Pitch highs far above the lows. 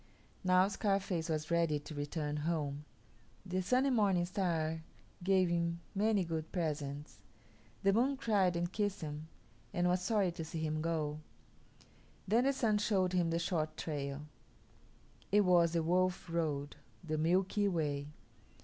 No: average, 3.6 semitones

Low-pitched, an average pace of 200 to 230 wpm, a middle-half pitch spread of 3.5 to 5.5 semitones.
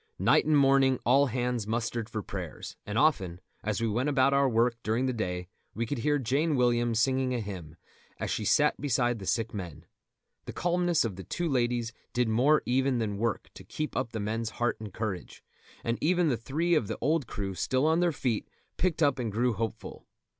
Yes: low, 120 Hz; fast, 205 wpm; average, 4.0 semitones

